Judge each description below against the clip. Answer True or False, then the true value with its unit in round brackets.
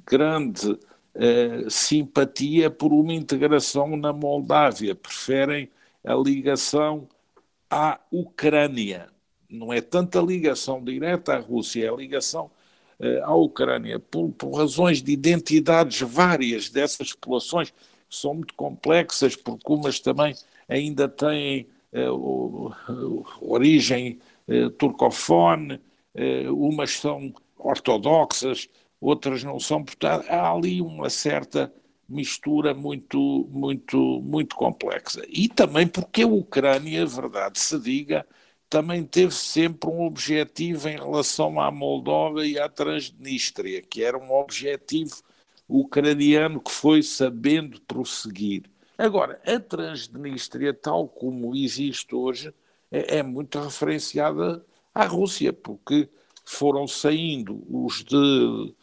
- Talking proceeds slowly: True (110 wpm)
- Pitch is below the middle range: False (145 Hz)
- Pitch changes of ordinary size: True (3.4 semitones)